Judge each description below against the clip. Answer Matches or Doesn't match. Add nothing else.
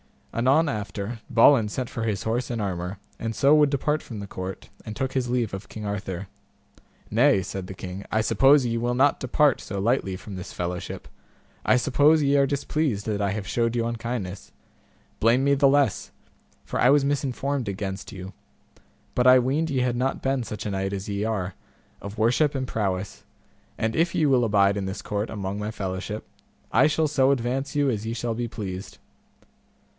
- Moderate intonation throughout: Matches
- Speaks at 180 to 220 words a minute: Matches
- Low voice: Matches